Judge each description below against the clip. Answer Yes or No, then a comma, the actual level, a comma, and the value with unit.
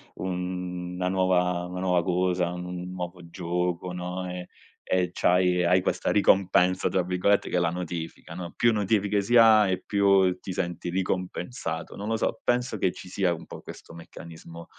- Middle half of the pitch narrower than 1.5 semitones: Yes, narrow, 1.1 semitones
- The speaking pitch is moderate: No, very low, 90 Hz